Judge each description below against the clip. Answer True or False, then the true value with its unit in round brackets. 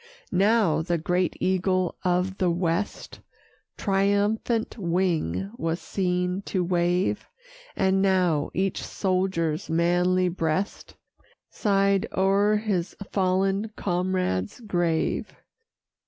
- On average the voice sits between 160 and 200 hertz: True (185 Hz)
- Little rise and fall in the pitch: True (2.1 semitones)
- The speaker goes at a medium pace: False (95 wpm)